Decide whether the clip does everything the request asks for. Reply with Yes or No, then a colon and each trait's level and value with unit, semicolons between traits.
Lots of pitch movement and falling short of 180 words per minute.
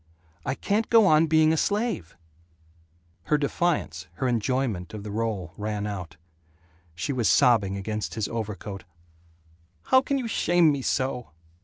Yes: wide, 7.9 semitones; average, 150 wpm